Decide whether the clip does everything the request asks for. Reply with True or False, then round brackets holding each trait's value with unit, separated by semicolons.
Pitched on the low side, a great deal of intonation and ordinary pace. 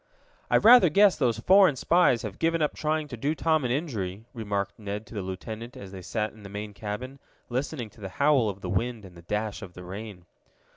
False (110 Hz; 6.2 semitones; 225 wpm)